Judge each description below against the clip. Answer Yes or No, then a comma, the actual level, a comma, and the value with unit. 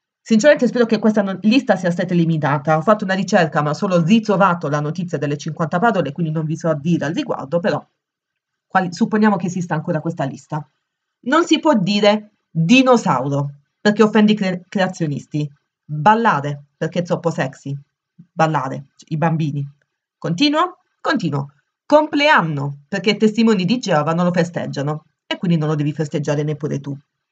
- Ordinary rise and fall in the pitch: No, wide, 5.9 semitones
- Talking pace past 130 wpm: Yes, average, 165 wpm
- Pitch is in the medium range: Yes, medium, 170 Hz